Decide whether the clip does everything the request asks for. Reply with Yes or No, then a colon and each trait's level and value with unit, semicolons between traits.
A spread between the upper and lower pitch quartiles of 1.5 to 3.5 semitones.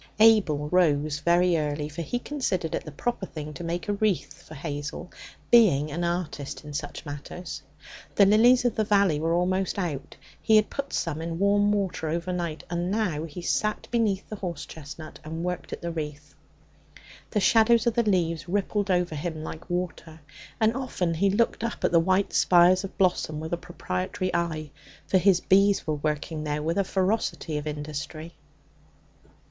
No: average, 4.4 semitones